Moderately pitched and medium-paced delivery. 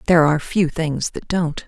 No: medium, 160 Hz; fast, 215 wpm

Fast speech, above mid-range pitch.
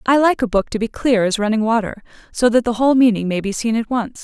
Yes: fast, 285 wpm; high, 230 Hz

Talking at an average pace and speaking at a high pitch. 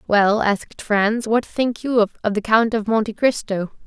Yes: average, 185 wpm; high, 220 Hz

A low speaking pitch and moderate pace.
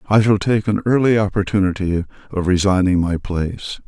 Yes: low, 100 Hz; average, 155 wpm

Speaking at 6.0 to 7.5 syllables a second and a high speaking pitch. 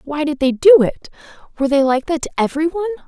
Yes: 7.2 syllables/s; very high, 280 Hz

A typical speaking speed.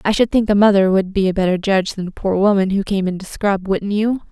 No: fast, 290 wpm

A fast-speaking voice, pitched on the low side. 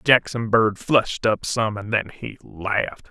No: average, 175 wpm; low, 110 Hz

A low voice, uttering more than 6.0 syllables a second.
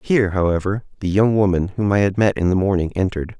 Yes: very low, 95 Hz; 6.4 syllables/s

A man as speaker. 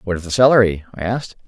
Yes: male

